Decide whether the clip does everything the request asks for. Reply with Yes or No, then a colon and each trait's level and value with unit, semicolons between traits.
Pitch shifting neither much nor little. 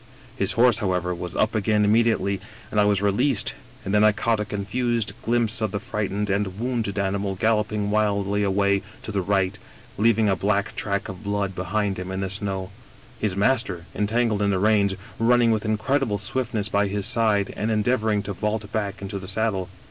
No: narrow, 1.8 semitones